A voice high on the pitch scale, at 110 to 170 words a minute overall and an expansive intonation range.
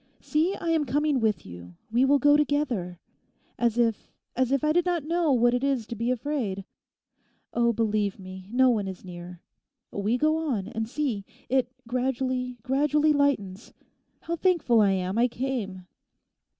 Yes: high, 245 Hz; average, 165 wpm; wide, 5.8 semitones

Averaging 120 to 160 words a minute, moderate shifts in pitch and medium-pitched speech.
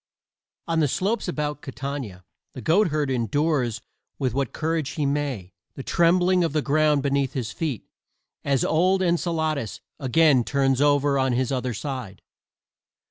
Yes: average, 140 wpm; average, 3.4 semitones; medium, 145 Hz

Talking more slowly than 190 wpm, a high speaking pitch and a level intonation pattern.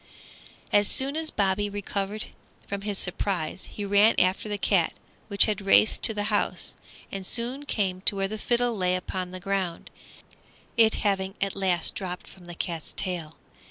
Yes: average, 170 wpm; high, 195 Hz; narrow, 2.2 semitones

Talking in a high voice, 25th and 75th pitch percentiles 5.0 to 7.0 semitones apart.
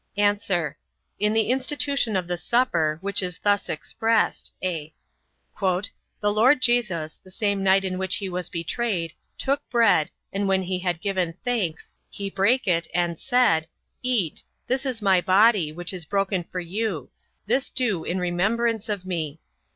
No: high, 195 Hz; average, 4.3 semitones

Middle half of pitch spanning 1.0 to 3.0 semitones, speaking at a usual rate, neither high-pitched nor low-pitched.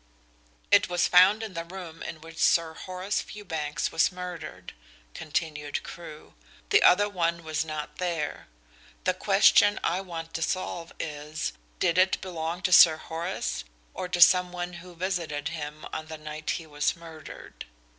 Yes: narrow, 2.4 semitones; average, 155 wpm; medium, 170 Hz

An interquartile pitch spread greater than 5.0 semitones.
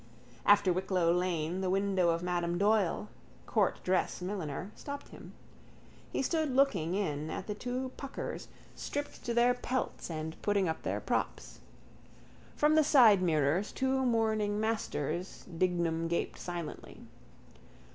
Yes: wide, 5.4 semitones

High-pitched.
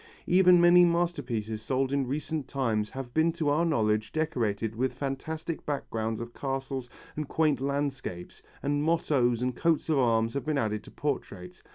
No: low, 135 Hz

